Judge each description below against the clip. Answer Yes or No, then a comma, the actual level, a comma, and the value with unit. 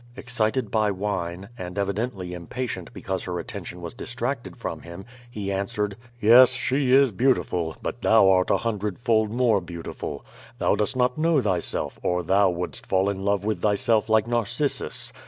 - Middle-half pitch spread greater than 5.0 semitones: No, average, 4.2 semitones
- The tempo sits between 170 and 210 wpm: Yes, average, 175 wpm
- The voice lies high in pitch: No, low, 105 Hz